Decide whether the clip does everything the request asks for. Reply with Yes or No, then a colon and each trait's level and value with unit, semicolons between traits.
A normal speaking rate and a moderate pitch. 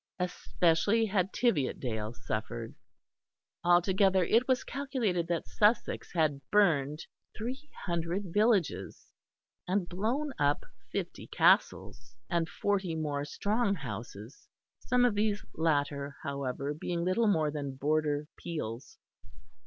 No: slow, 110 wpm; medium, 170 Hz